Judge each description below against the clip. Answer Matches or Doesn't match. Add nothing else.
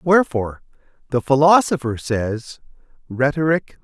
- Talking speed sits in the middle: Doesn't match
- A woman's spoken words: Doesn't match